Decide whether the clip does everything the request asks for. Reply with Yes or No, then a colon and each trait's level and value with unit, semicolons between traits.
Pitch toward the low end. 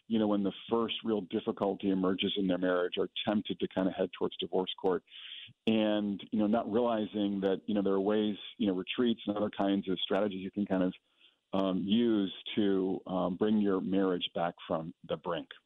Yes: low, 100 Hz